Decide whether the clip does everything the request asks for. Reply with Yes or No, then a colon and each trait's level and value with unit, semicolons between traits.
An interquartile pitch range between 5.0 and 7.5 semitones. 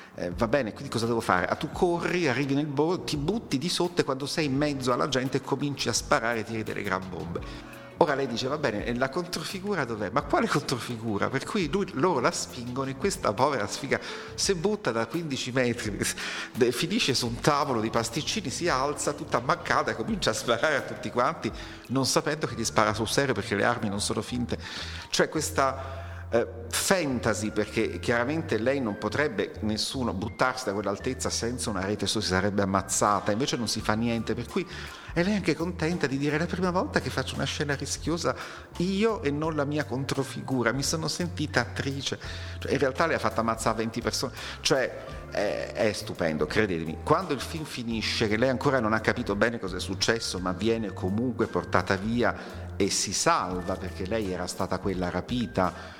Yes: wide, 5.5 semitones